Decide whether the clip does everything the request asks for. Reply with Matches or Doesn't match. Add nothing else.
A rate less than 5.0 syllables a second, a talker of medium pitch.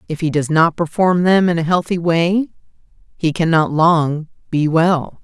Matches